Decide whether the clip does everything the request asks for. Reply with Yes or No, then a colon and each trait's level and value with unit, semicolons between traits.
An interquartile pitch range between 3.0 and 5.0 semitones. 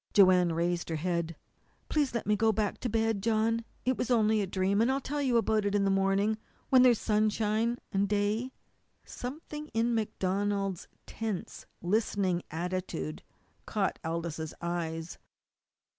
Yes: average, 3.8 semitones